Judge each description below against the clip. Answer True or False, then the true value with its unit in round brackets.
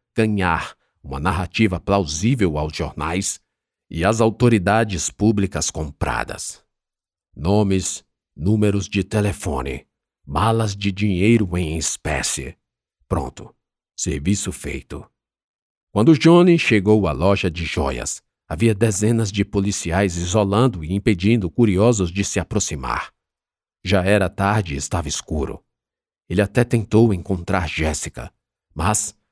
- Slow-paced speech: True (110 wpm)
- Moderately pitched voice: False (100 Hz)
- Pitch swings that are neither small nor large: True (3.9 semitones)